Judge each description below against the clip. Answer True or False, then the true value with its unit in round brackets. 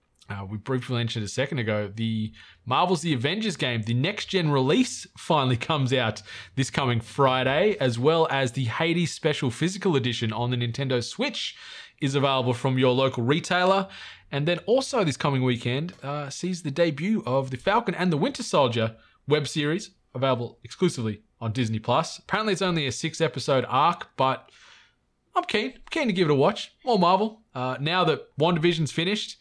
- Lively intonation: True (6.1 semitones)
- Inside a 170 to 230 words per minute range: True (175 wpm)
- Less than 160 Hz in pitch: True (140 Hz)